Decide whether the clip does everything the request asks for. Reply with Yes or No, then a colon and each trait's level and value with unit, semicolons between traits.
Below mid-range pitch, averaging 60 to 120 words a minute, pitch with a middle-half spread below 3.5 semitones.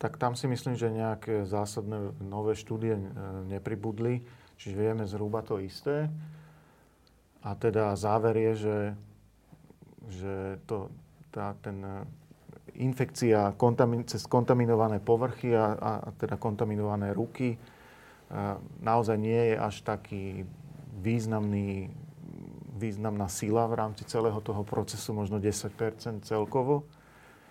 Yes: low, 110 Hz; slow, 110 wpm; narrow, 2.6 semitones